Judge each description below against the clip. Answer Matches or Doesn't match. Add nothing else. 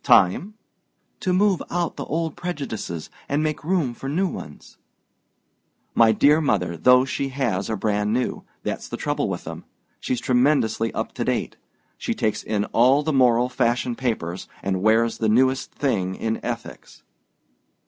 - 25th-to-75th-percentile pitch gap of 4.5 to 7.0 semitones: Matches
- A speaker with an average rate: Matches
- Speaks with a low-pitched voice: Matches